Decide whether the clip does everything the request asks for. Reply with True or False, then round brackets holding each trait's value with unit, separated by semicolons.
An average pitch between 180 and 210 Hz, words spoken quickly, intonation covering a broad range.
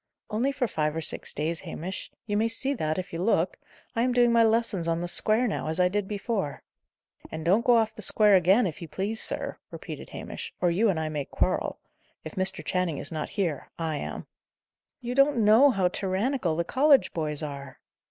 True (190 Hz; 210 wpm; 5.9 semitones)